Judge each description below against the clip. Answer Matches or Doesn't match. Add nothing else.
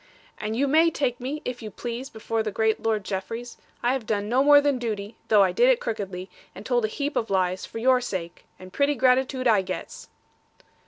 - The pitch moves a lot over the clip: Doesn't match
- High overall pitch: Matches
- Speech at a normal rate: Doesn't match